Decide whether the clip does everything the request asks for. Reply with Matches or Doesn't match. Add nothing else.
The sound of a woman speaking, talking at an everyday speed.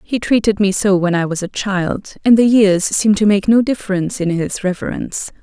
Doesn't match